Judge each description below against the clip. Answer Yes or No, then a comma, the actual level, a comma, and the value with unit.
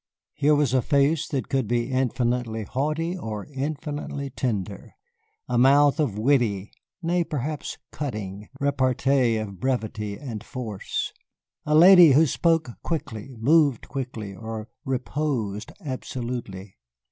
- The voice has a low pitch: Yes, low, 130 Hz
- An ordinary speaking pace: No, slow, 120 wpm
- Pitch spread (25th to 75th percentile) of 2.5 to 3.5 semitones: No, average, 4.8 semitones